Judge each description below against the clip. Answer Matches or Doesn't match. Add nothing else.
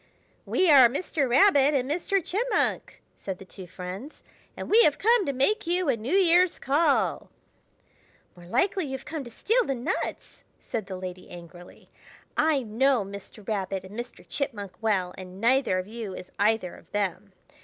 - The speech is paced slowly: Doesn't match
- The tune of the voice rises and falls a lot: Matches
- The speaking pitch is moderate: Doesn't match